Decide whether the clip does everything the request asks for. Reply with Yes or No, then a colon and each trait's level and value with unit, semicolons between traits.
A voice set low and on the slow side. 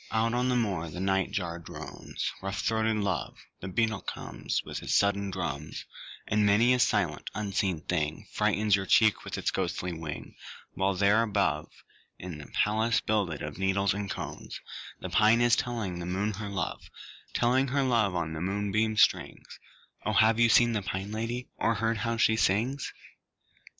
No: low, 100 Hz; average, 175 wpm